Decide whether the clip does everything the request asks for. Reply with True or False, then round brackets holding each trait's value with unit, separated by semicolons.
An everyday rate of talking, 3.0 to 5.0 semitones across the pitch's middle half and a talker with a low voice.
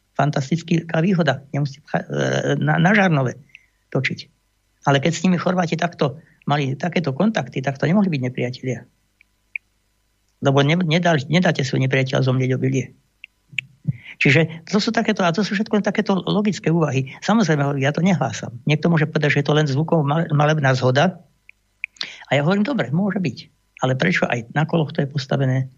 False (150 wpm; 4.7 semitones; 145 Hz)